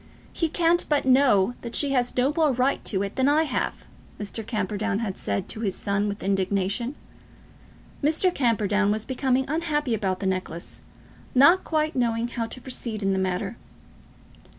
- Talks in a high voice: Yes, high, 235 Hz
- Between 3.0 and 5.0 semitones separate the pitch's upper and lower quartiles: No, wide, 5.6 semitones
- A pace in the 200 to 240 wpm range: No, average, 170 wpm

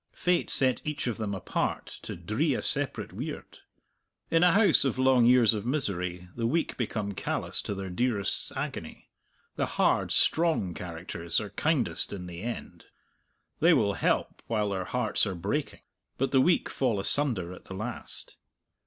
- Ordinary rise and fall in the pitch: No, wide, 5.7 semitones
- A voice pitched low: Yes, low, 115 Hz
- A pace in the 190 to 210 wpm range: No, average, 165 wpm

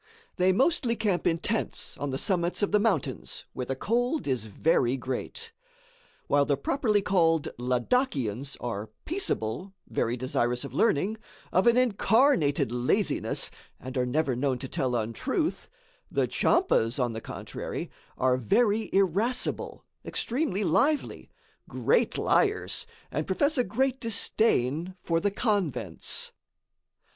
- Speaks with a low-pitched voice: No, medium, 175 Hz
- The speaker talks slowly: Yes, slow, 130 wpm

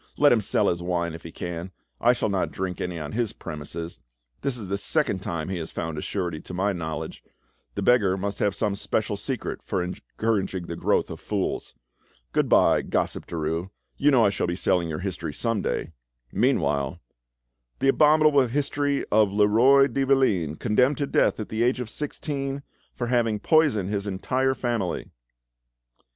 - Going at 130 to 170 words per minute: No, average, 180 wpm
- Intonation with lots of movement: Yes, wide, 6.3 semitones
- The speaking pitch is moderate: No, low, 100 Hz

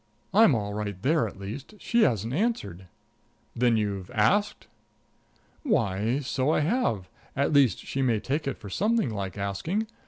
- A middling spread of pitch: No, wide, 7.7 semitones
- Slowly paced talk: No, average, 155 wpm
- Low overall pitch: Yes, low, 125 Hz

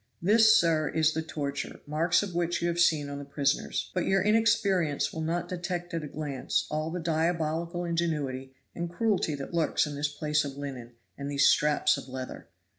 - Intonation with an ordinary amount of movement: Yes, average, 3.3 semitones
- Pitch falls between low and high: Yes, medium, 160 Hz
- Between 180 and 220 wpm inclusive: Yes, average, 190 wpm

